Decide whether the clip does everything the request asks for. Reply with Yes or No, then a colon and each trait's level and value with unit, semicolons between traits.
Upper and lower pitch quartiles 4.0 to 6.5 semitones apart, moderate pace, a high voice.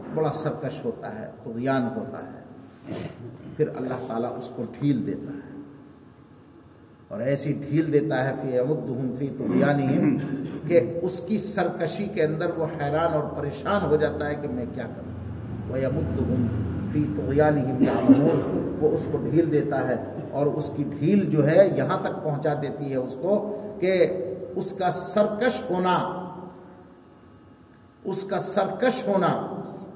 No: average, 5.1 semitones; average, 145 wpm; medium, 150 Hz